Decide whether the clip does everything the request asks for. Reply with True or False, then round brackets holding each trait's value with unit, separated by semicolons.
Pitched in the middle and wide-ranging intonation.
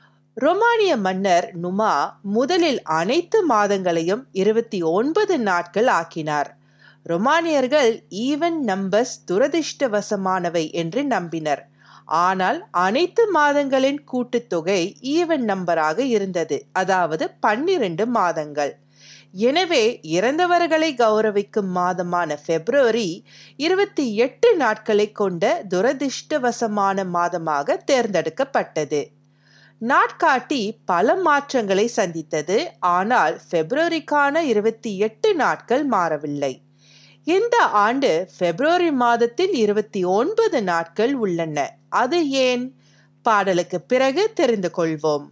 False (215 Hz; 8.4 semitones)